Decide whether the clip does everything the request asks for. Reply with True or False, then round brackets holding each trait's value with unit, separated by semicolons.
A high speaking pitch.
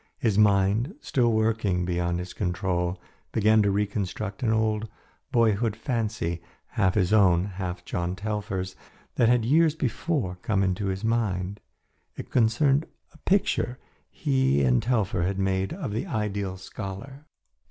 False (105 Hz)